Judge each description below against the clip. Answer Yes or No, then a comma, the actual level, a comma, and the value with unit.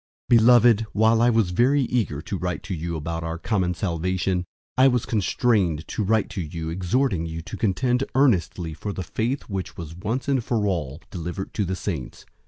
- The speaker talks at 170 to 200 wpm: Yes, average, 190 wpm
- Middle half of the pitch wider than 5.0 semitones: Yes, wide, 5.4 semitones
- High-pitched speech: No, very low, 95 Hz